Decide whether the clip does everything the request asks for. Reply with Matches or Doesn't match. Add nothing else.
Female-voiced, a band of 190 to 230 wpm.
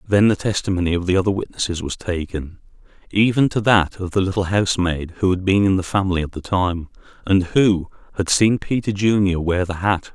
Doesn't match